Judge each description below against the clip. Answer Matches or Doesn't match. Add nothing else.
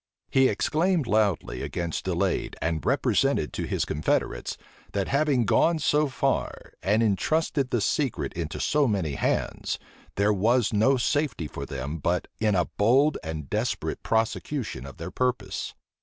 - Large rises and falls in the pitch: Matches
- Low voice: Matches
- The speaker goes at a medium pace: Matches